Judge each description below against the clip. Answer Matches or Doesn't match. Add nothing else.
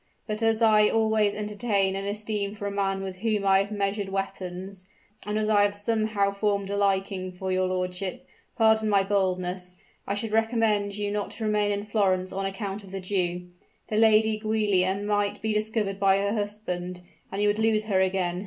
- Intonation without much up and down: Matches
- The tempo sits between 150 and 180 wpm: Doesn't match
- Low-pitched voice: Doesn't match